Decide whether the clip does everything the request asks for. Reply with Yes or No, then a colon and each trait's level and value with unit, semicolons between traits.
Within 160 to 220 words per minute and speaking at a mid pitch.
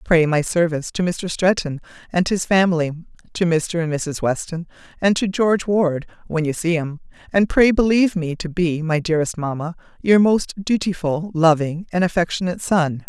Yes: average, 175 wpm; medium, 170 Hz